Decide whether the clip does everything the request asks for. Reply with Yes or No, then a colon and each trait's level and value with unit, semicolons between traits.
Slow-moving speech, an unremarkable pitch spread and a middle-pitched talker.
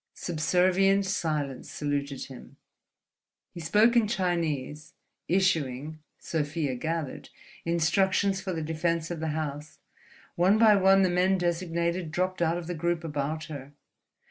Yes: slow, 130 wpm; average, 3.3 semitones; medium, 170 Hz